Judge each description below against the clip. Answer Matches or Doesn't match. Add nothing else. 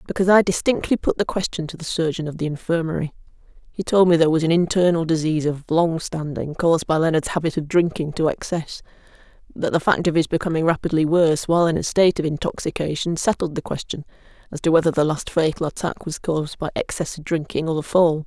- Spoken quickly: Matches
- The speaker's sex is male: Doesn't match